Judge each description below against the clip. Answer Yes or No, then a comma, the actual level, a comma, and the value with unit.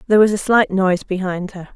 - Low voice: No, high, 195 Hz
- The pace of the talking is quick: Yes, fast, 240 wpm